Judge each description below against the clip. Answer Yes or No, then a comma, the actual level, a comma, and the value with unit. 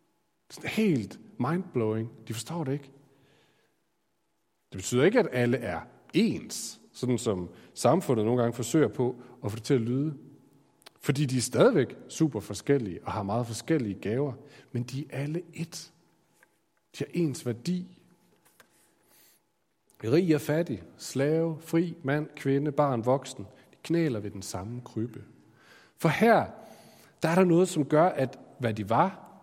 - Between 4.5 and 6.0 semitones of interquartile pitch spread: Yes, average, 5.1 semitones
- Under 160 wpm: Yes, average, 150 wpm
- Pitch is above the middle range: No, medium, 140 Hz